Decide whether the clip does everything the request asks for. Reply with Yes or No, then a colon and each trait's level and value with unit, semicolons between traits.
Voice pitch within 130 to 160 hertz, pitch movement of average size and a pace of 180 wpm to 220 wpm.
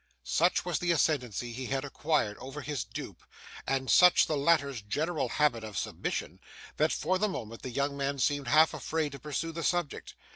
Yes: medium, 140 Hz; average, 3.7 semitones; average, 185 wpm